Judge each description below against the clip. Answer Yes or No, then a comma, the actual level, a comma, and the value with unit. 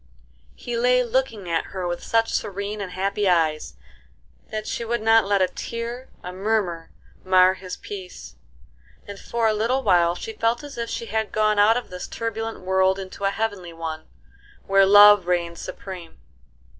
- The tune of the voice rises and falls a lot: No, average, 3.6 semitones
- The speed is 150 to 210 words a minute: Yes, average, 170 wpm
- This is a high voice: Yes, high, 200 Hz